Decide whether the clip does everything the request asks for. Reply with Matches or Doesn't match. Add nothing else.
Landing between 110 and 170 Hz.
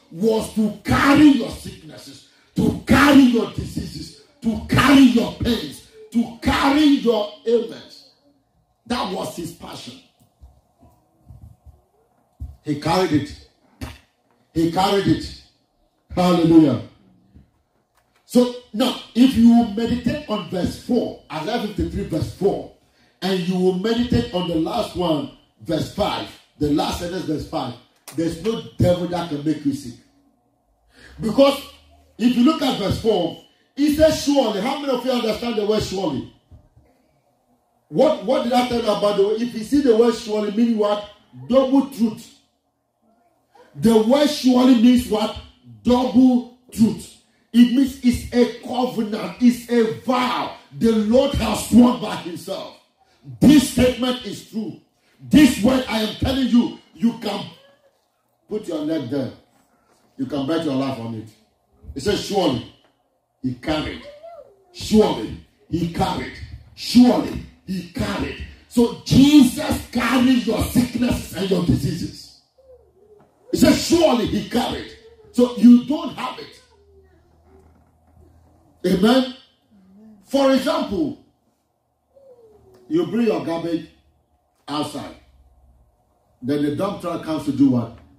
Doesn't match